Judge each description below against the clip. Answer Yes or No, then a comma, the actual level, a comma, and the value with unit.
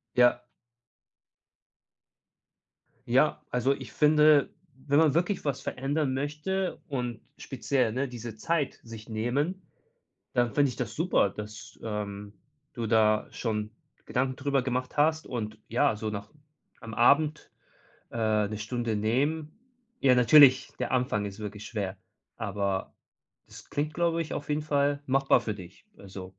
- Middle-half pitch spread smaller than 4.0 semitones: No, average, 5.1 semitones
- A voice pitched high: No, low, 125 Hz